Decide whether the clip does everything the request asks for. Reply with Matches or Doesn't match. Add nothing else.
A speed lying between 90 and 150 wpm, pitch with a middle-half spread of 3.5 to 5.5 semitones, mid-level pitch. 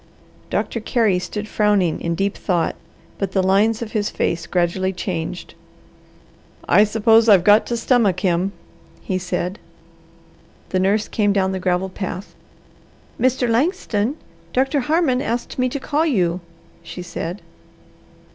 Doesn't match